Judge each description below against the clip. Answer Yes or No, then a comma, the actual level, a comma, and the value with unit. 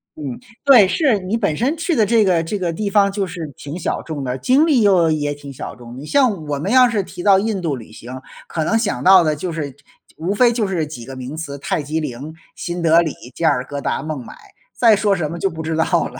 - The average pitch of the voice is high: No, medium, 170 Hz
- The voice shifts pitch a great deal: Yes, wide, 5.9 semitones